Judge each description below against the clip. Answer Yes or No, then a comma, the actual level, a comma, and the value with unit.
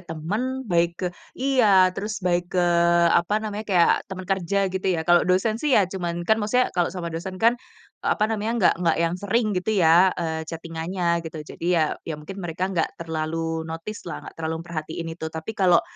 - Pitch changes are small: No, average, 3.6 semitones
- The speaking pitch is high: No, medium, 175 Hz